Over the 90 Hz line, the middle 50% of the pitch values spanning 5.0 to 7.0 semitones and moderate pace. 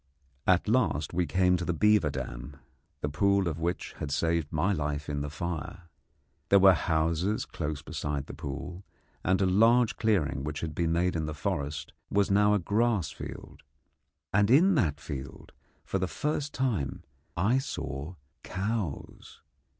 No: very low, 85 Hz; wide, 5.4 semitones; average, 160 wpm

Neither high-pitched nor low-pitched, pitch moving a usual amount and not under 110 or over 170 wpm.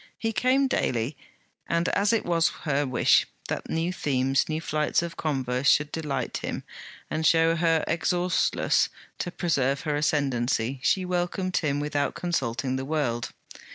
Yes: medium, 155 Hz; average, 4.1 semitones; average, 150 wpm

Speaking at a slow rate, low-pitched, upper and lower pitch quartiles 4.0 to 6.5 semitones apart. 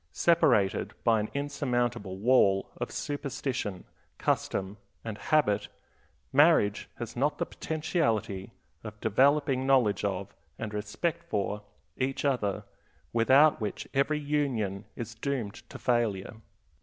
Yes: slow, 115 wpm; low, 120 Hz; average, 5.3 semitones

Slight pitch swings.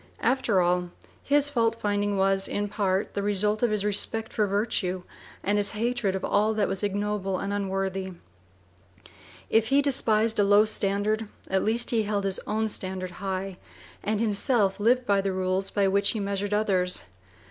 Yes: narrow, 2.0 semitones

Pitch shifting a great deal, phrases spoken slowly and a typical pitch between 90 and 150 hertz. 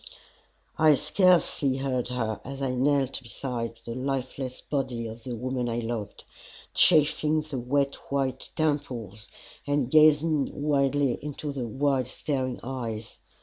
No: average, 2.8 semitones; slow, 130 wpm; low, 135 Hz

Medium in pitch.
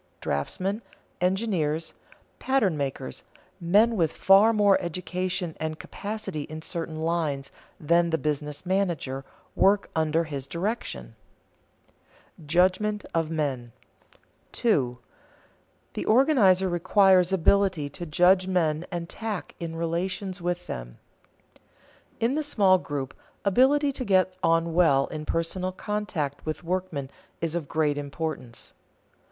Yes: medium, 175 Hz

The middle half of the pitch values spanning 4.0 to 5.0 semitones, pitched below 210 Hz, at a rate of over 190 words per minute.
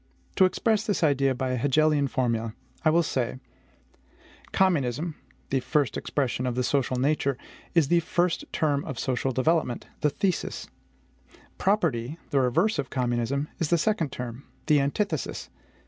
No: average, 4.5 semitones; medium, 140 Hz; average, 145 wpm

